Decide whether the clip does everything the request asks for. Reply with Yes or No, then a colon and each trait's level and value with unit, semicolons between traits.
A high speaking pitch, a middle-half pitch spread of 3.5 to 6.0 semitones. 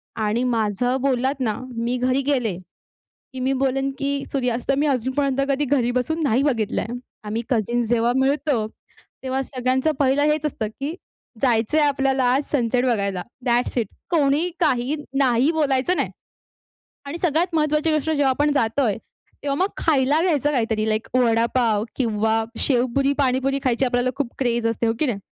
No: very high, 260 Hz; average, 3.1 semitones